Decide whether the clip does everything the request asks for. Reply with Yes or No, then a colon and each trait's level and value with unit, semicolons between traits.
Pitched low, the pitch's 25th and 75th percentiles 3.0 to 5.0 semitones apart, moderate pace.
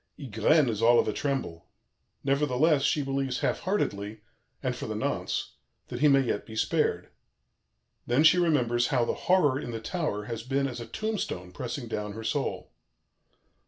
Yes: low, 125 Hz; average, 4.6 semitones; average, 170 wpm